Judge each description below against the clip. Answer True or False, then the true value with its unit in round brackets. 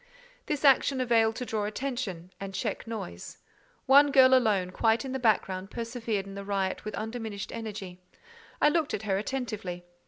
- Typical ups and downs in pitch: True (4.4 semitones)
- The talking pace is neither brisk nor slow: True (165 wpm)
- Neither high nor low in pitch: False (220 Hz)